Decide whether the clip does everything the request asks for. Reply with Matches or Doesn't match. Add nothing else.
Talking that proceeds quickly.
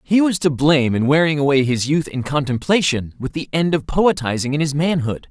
Matches